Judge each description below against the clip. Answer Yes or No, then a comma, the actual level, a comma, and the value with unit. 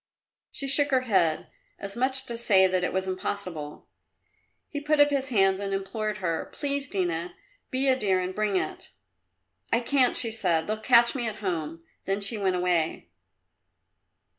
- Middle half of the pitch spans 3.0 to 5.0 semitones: No, wide, 5.6 semitones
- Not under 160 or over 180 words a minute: Yes, average, 175 wpm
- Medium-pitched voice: No, high, 200 Hz